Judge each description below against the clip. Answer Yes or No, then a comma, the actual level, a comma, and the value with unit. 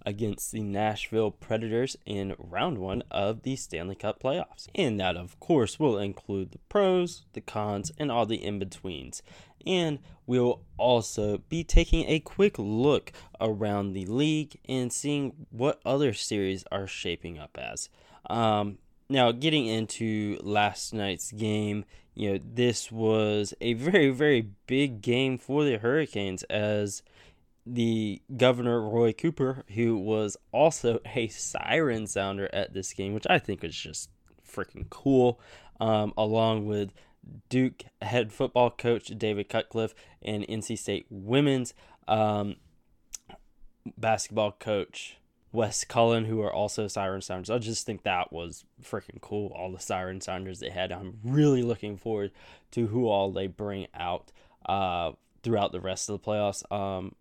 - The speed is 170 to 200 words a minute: No, average, 150 wpm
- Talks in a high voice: No, low, 110 Hz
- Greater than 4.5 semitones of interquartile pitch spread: No, average, 3.7 semitones